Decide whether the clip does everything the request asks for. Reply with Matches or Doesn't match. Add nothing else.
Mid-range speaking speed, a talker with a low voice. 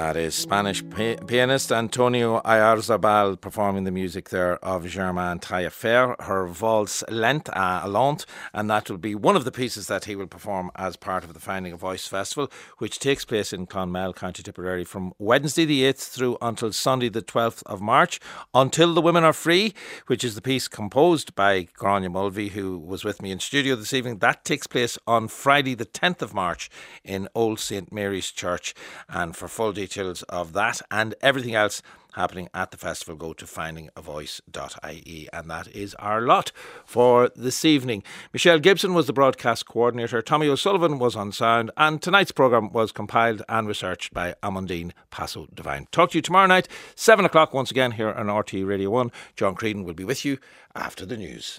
Matches